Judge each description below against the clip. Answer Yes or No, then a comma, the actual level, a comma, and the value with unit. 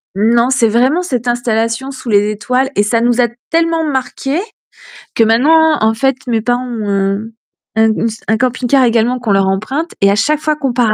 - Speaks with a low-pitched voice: No, high, 240 Hz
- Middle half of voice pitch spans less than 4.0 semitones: Yes, average, 3.3 semitones